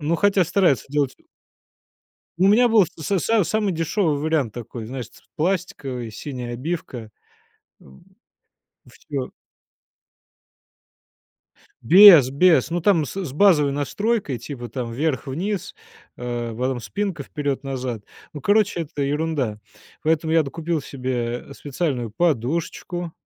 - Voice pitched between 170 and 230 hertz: No, medium, 150 Hz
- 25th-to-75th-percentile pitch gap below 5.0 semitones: No, wide, 5.4 semitones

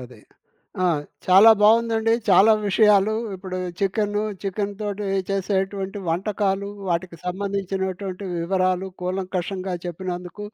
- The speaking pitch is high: Yes, high, 195 Hz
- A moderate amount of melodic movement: No, narrow, 1.9 semitones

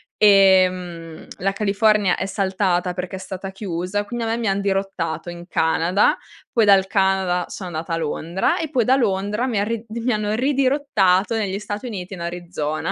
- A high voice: Yes, high, 195 Hz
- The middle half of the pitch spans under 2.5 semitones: No, average, 2.9 semitones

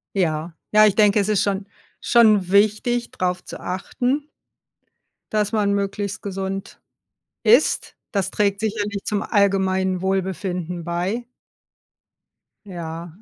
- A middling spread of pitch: No, narrow, 2.2 semitones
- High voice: Yes, high, 200 Hz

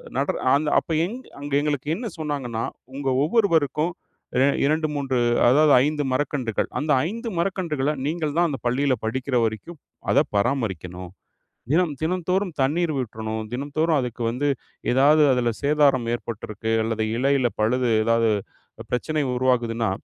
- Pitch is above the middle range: No, medium, 140 Hz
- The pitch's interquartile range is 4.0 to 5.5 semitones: Yes, average, 4.4 semitones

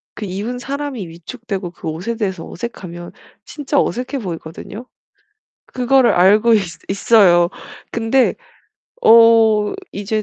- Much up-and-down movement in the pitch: No, average, 4.5 semitones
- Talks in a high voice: Yes, high, 215 Hz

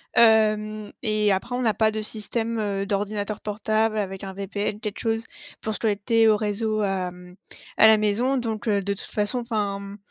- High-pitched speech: Yes, high, 215 Hz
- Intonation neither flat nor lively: No, narrow, 1.6 semitones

